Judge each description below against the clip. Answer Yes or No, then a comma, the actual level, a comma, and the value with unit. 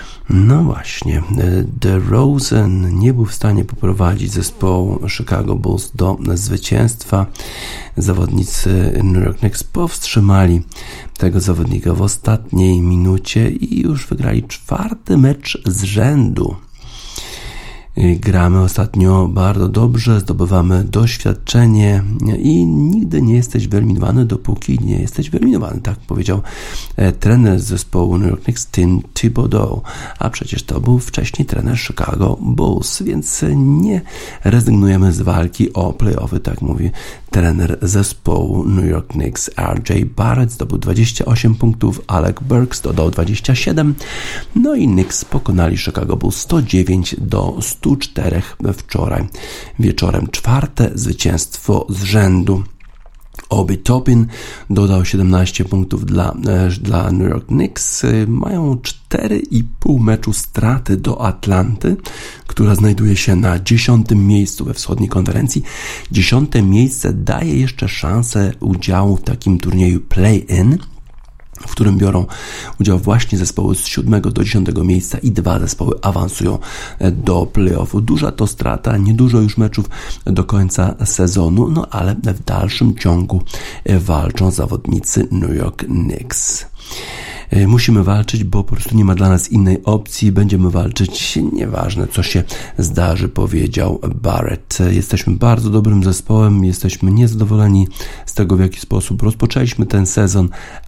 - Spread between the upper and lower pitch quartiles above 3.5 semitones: Yes, average, 3.9 semitones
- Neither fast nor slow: Yes, average, 125 wpm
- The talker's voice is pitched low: Yes, low, 100 Hz